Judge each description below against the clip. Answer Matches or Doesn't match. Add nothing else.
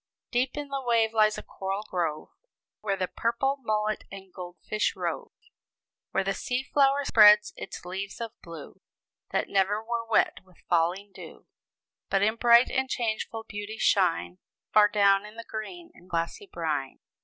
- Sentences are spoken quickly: Doesn't match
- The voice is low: Doesn't match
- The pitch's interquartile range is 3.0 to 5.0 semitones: Matches